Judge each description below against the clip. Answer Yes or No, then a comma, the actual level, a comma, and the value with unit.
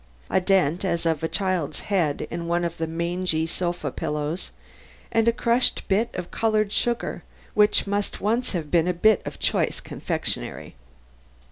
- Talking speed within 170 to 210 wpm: No, average, 160 wpm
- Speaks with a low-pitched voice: No, medium, 180 Hz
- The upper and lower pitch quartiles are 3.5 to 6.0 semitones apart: Yes, average, 4.0 semitones